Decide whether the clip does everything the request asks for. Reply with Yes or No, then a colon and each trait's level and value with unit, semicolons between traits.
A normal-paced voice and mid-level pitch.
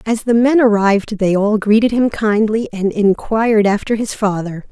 No: average, 180 wpm; high, 215 Hz